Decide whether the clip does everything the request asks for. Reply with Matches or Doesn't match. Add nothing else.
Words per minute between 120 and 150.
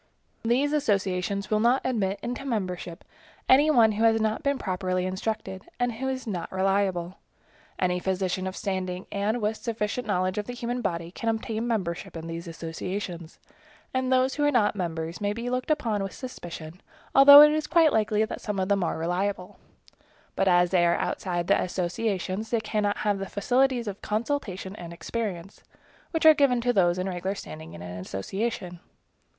Doesn't match